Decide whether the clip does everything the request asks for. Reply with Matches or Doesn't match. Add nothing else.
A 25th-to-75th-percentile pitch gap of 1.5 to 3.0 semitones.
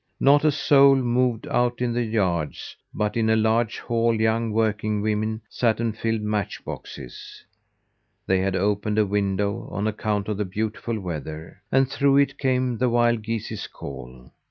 Matches